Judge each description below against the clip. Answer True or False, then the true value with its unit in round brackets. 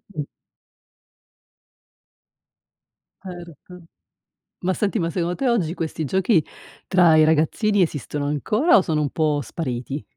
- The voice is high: False (170 Hz)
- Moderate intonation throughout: True (3.7 semitones)